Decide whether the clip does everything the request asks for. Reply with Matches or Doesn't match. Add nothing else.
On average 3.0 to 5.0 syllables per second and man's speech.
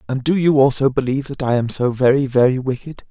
Doesn't match